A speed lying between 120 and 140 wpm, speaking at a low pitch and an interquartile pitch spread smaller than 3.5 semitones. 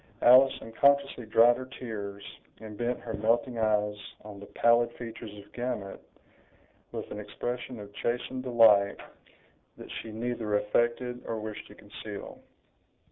Yes: slow, 135 wpm; low, 115 Hz; average, 2.7 semitones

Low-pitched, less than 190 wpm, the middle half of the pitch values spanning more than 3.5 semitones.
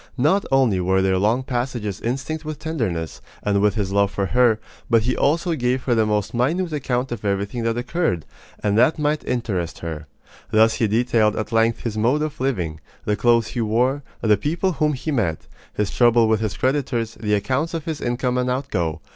No: low, 120 Hz; average, 195 wpm; average, 4.3 semitones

